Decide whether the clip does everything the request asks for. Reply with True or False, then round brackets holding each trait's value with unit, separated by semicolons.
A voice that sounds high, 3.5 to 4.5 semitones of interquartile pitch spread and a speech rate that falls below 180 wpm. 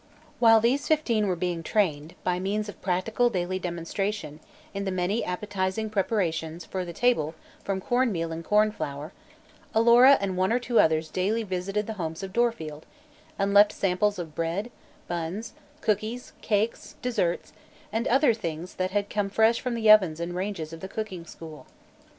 True (195 Hz; 4.1 semitones; 170 wpm)